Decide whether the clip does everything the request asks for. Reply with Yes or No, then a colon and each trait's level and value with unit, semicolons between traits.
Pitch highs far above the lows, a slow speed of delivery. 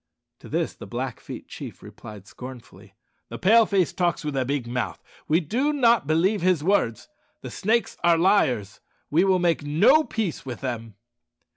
No: wide, 7.7 semitones; average, 165 wpm